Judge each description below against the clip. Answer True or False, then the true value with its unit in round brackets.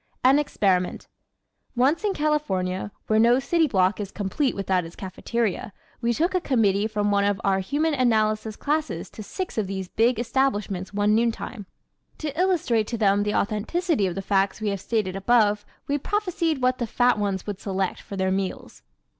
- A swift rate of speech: False (180 wpm)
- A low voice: False (215 Hz)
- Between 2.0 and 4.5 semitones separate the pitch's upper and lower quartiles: False (5.2 semitones)